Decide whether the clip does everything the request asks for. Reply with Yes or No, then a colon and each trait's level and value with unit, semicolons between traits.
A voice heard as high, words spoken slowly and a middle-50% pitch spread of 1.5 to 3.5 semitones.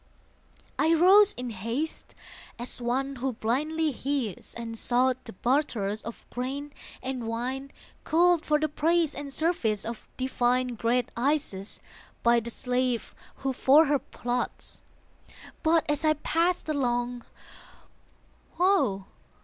No: very high, 260 Hz; slow, 125 wpm; average, 4.4 semitones